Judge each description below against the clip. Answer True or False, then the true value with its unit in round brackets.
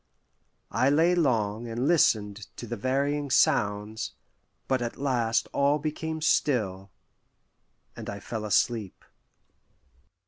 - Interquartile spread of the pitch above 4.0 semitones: True (5.2 semitones)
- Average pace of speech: False (110 wpm)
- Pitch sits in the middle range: False (120 Hz)